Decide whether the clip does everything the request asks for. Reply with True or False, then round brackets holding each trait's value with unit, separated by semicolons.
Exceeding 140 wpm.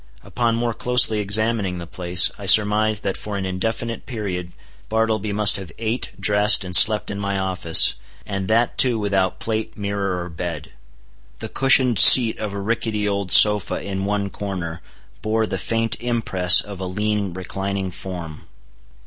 True (160 wpm)